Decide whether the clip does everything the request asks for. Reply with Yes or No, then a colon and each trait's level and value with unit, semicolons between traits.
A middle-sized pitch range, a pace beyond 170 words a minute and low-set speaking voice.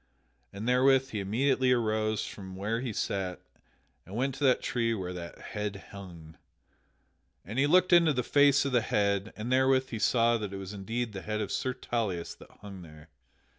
Yes: average, 4.7 semitones; average, 190 wpm; low, 110 Hz